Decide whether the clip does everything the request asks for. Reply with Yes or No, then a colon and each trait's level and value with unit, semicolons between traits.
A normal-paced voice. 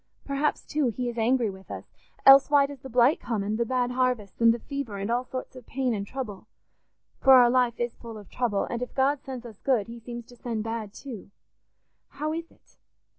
No: fast, 225 wpm